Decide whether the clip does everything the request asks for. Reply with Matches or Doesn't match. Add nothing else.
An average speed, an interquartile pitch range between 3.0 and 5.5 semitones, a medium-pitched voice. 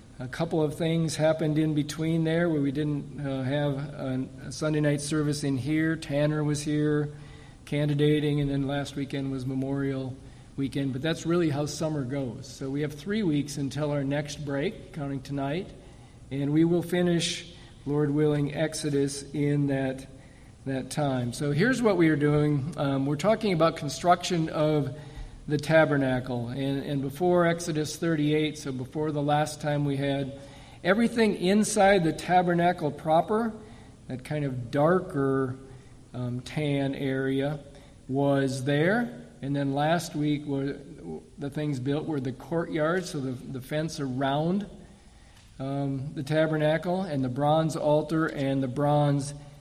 Doesn't match